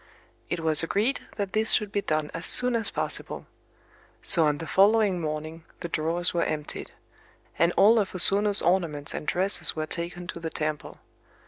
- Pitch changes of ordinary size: Yes, average, 4.2 semitones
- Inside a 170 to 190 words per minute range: Yes, average, 180 wpm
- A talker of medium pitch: Yes, medium, 175 Hz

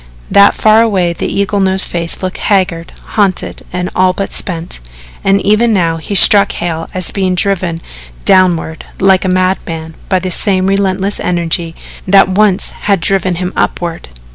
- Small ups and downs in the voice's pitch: Yes, narrow, 2.3 semitones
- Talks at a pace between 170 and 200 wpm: No, average, 160 wpm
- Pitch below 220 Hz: Yes, medium, 185 Hz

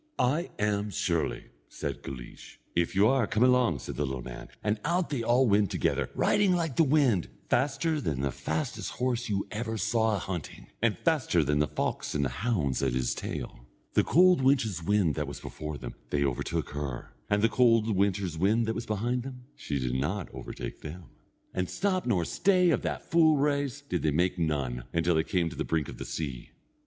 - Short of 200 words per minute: No, fast, 205 wpm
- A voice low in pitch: Yes, low, 105 Hz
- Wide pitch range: Yes, wide, 8.7 semitones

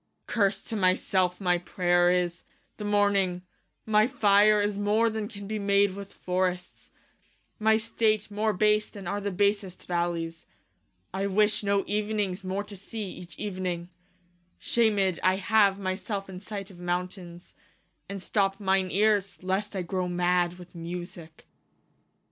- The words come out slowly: No, average, 155 wpm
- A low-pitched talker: No, high, 195 Hz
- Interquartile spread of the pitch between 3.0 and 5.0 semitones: No, narrow, 2.4 semitones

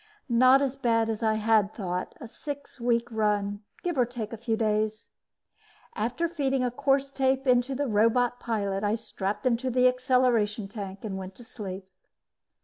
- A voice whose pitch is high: Yes, high, 230 Hz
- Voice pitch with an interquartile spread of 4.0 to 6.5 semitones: No, average, 3.3 semitones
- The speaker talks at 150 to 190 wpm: Yes, average, 170 wpm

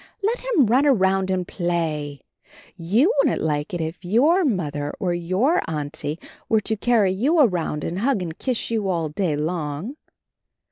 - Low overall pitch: No, medium, 185 Hz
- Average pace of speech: Yes, average, 170 wpm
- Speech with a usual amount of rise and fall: No, wide, 7.1 semitones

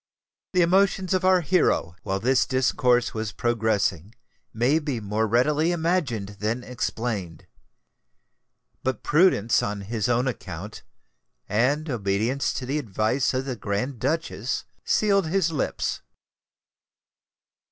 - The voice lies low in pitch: Yes, low, 125 Hz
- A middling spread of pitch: No, wide, 6.0 semitones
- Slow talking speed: Yes, slow, 120 wpm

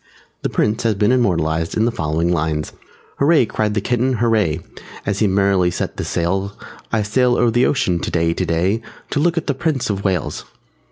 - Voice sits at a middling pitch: No, low, 105 Hz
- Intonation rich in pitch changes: Yes, wide, 5.7 semitones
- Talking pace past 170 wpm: Yes, average, 185 wpm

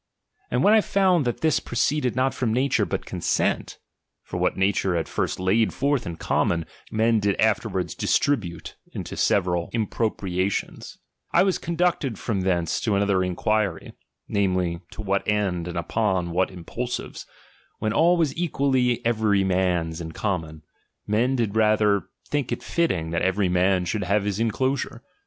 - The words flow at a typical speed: Yes, average, 160 wpm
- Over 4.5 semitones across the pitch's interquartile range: Yes, average, 5.2 semitones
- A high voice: No, low, 105 Hz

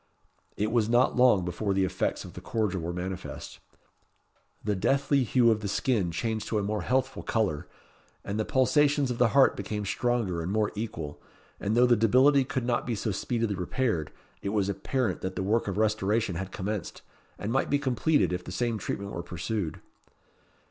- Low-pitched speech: Yes, low, 110 Hz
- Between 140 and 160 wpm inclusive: No, average, 190 wpm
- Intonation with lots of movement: No, average, 4.2 semitones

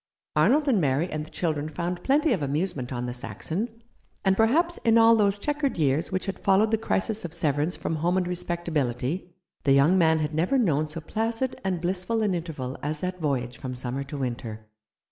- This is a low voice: No, medium, 170 Hz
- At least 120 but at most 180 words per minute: No, average, 200 wpm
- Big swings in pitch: Yes, wide, 6.0 semitones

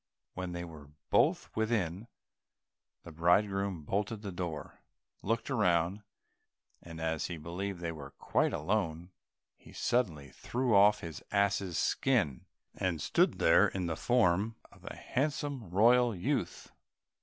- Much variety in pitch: No, average, 4.7 semitones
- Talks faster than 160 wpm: No, slow, 135 wpm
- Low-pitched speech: Yes, very low, 95 Hz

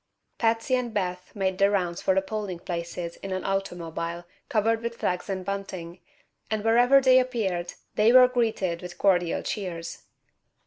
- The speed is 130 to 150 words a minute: No, average, 160 wpm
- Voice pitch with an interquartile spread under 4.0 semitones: No, average, 4.3 semitones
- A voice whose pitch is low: No, high, 195 Hz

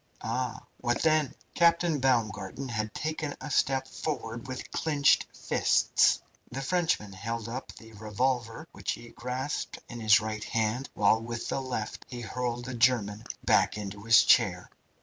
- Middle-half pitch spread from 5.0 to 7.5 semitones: No, average, 3.4 semitones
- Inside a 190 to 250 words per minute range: No, average, 150 wpm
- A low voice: Yes, low, 120 Hz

